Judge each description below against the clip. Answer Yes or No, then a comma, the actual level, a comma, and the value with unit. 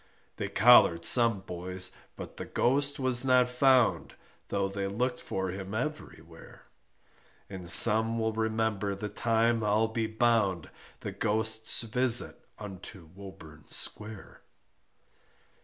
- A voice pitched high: No, low, 110 Hz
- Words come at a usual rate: No, slow, 120 wpm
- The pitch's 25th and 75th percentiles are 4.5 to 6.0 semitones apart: No, average, 3.4 semitones